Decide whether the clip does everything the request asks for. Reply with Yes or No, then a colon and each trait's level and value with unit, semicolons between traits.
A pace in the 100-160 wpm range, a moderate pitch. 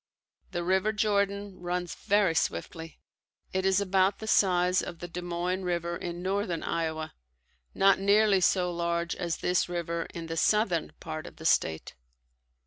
Yes: average, 155 wpm; medium, 180 Hz